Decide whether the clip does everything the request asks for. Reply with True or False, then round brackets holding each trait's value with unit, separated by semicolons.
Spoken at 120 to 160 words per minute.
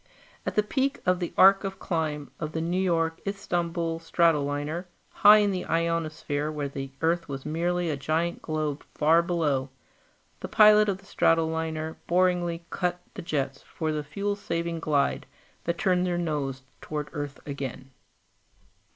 True (155 wpm)